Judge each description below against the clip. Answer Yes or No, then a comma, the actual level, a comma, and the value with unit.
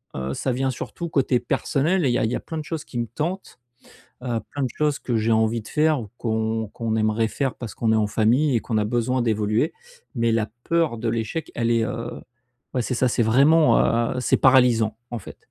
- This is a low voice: Yes, low, 120 Hz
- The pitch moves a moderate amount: Yes, average, 3.3 semitones